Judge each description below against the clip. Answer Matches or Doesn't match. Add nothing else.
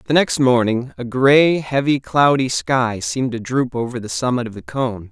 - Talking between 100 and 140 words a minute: Doesn't match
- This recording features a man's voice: Matches